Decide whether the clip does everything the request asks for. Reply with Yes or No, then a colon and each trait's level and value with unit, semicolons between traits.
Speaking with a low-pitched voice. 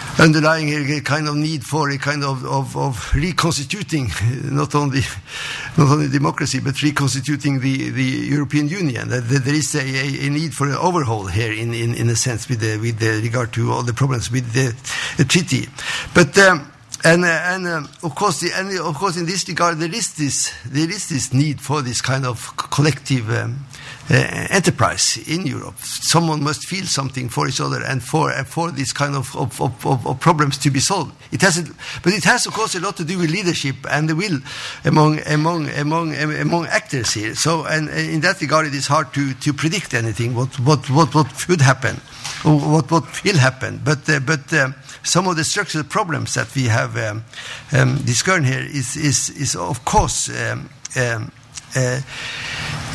No: medium, 145 Hz